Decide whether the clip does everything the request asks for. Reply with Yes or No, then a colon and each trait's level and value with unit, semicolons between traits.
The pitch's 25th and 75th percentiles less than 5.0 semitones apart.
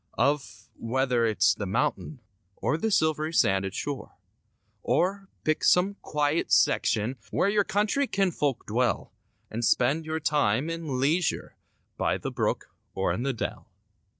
No: wide, 5.6 semitones